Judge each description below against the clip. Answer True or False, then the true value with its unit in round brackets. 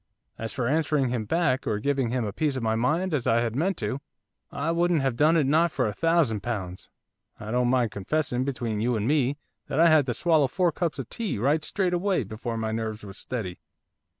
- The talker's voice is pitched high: False (130 Hz)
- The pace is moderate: False (225 wpm)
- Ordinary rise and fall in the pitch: False (5.7 semitones)